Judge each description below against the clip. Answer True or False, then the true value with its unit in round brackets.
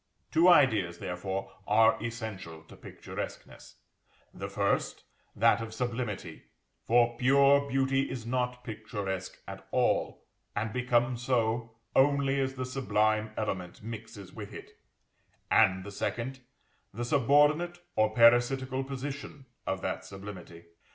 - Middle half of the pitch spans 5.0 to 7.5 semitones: False (4.2 semitones)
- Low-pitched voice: True (115 Hz)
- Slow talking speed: True (120 wpm)